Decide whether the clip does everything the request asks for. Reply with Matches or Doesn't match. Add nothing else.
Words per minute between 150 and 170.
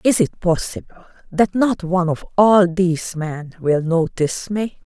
Matches